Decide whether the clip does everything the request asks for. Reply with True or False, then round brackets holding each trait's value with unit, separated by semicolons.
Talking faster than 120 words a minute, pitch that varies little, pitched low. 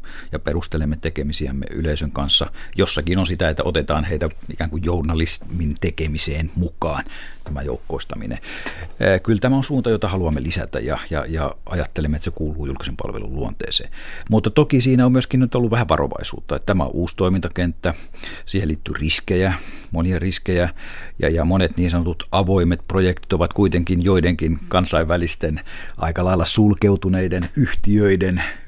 False (145 wpm; 3.4 semitones; 85 Hz)